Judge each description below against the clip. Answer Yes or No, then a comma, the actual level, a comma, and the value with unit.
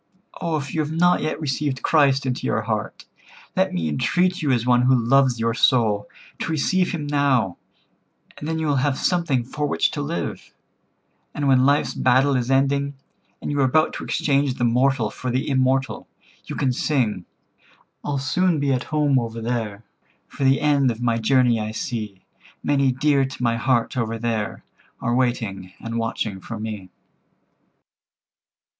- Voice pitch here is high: No, low, 130 Hz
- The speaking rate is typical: Yes, average, 175 wpm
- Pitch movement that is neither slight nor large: Yes, average, 3.6 semitones